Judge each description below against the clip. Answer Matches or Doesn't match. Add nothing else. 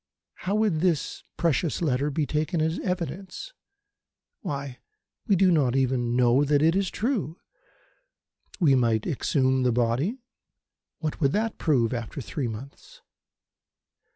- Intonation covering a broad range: Matches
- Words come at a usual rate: Doesn't match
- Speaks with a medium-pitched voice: Matches